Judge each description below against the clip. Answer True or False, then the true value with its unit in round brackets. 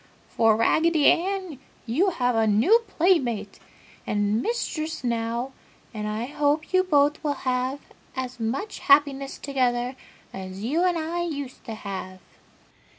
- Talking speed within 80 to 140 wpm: True (135 wpm)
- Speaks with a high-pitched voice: True (270 Hz)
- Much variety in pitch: True (5.8 semitones)